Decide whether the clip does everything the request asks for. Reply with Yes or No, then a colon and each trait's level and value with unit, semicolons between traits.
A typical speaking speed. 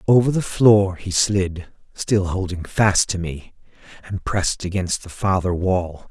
Yes: average, 155 wpm